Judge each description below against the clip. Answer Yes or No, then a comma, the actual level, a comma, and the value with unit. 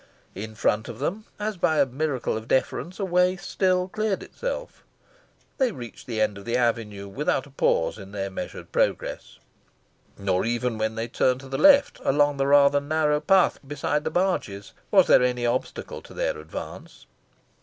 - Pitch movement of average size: No, wide, 8.0 semitones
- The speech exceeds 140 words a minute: Yes, average, 175 wpm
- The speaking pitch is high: No, low, 135 Hz